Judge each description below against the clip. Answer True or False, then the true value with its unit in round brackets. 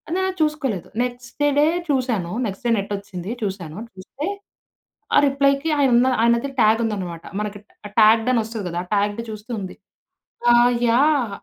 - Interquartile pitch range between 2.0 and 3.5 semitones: False (4.8 semitones)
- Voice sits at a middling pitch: False (225 Hz)